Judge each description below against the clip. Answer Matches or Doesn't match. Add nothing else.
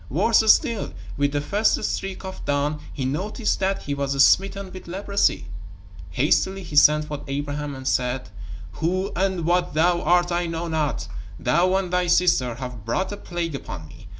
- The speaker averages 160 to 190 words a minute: Matches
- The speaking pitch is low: Doesn't match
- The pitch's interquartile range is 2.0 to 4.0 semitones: Doesn't match